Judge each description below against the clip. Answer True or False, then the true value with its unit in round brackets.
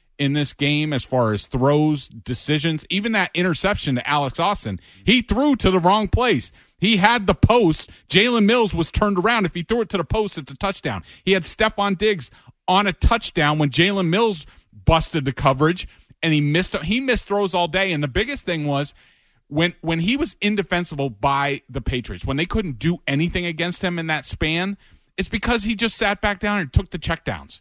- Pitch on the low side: False (170 Hz)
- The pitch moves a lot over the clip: True (6.0 semitones)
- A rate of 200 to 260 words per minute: True (205 wpm)